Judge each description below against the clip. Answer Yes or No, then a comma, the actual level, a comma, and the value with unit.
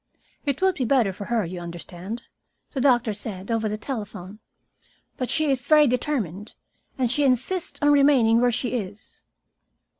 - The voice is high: Yes, high, 240 Hz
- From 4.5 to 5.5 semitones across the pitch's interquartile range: Yes, average, 4.9 semitones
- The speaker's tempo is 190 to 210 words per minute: No, average, 160 wpm